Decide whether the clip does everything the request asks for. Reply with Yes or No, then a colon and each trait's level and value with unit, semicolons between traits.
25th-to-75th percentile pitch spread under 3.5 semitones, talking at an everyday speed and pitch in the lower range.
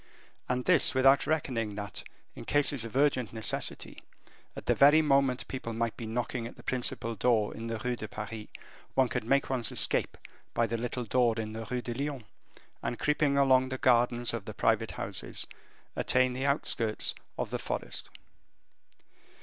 Yes: average, 2.8 semitones; average, 175 wpm; low, 125 Hz